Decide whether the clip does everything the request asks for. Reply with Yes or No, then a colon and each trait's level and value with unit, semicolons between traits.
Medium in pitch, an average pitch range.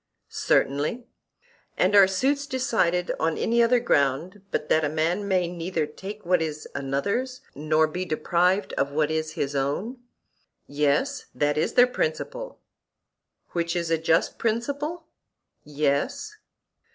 No: medium, 170 Hz; wide, 6.8 semitones